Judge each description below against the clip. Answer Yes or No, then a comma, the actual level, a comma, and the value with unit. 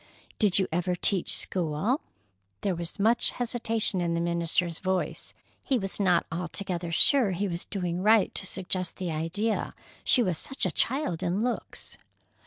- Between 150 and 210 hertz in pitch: Yes, medium, 185 Hz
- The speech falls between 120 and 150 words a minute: No, average, 160 wpm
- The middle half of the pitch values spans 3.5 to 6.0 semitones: Yes, average, 3.8 semitones